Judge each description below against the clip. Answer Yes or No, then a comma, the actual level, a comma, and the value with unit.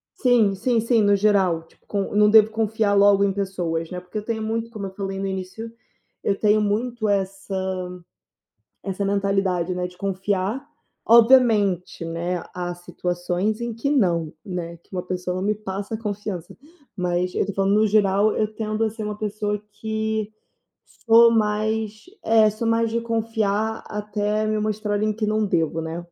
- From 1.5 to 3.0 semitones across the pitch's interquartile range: Yes, narrow, 2.6 semitones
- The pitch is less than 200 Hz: No, high, 205 Hz